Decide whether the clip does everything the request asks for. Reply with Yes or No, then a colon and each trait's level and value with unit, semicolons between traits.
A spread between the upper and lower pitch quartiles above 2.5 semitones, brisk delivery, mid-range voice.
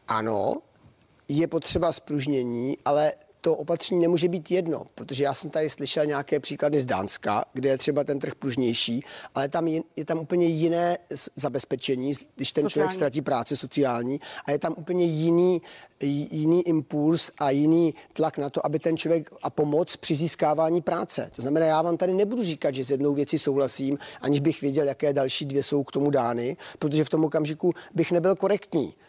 Yes: average, 2.9 semitones; fast, 180 wpm; medium, 150 Hz